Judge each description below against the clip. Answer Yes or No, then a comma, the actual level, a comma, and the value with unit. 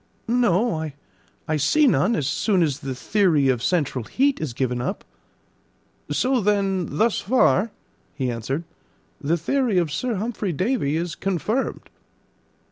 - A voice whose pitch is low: No, medium, 180 Hz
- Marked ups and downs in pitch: Yes, wide, 7.7 semitones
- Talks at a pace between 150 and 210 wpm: No, slow, 135 wpm